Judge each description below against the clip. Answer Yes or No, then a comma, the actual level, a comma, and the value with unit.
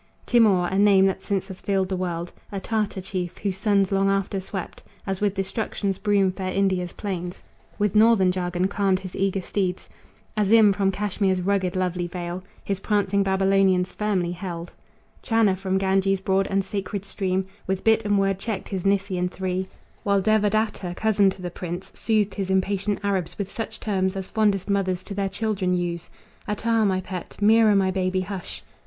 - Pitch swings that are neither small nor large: No, narrow, 1.6 semitones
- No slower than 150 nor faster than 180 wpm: Yes, average, 175 wpm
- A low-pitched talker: No, high, 195 Hz